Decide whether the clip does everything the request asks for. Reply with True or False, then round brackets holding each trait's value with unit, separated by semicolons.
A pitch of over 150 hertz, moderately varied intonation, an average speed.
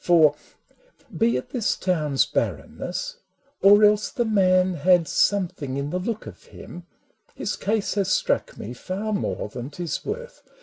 True (190 Hz; 4.7 semitones; 170 wpm)